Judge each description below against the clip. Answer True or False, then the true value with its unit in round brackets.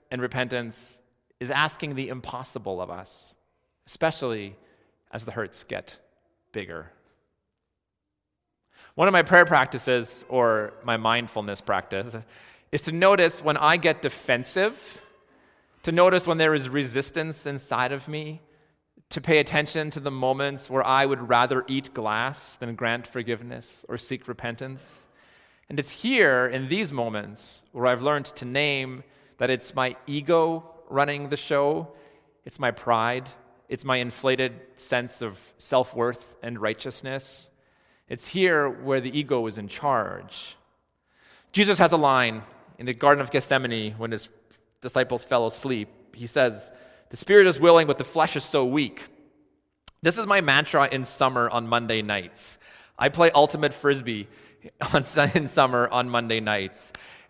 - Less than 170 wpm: True (145 wpm)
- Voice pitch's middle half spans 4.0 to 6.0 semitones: False (3.6 semitones)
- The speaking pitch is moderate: False (130 Hz)